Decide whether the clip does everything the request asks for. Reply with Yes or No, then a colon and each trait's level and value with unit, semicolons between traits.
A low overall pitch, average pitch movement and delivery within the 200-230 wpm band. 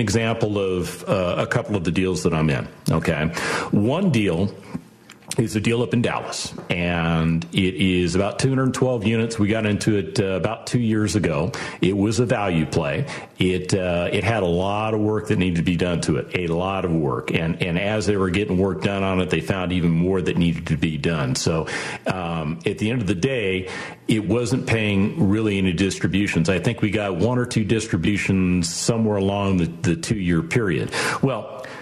Yes: very low, 95 Hz; average, 3.3 semitones; fast, 205 wpm